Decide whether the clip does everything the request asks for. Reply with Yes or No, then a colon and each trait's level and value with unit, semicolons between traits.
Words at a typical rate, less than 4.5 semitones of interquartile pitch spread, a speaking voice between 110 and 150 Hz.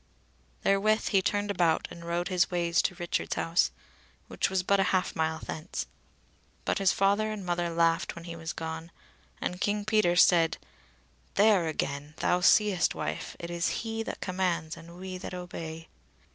No: average, 170 wpm; average, 2.8 semitones; medium, 175 Hz